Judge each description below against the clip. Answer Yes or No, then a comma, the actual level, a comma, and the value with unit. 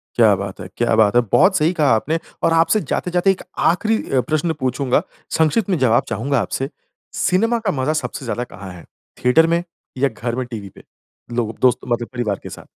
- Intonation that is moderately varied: No, wide, 6.1 semitones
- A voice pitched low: Yes, low, 130 Hz